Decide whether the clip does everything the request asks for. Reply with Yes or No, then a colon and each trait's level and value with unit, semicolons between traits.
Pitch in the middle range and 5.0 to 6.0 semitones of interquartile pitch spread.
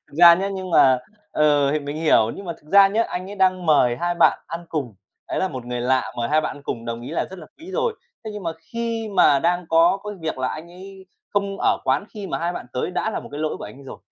Yes: medium, 170 Hz; wide, 5.4 semitones